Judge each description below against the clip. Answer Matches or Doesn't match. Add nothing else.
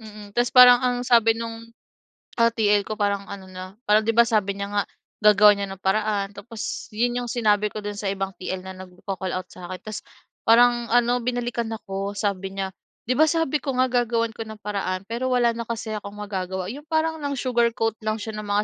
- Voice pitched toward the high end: Matches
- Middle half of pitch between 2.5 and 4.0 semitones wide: Matches